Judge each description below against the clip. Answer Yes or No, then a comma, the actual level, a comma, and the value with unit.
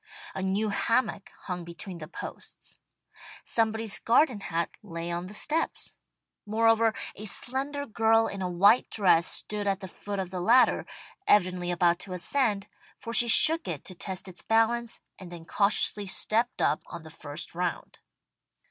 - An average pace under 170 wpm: Yes, average, 160 wpm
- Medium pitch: No, high, 200 Hz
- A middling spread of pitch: Yes, average, 4.2 semitones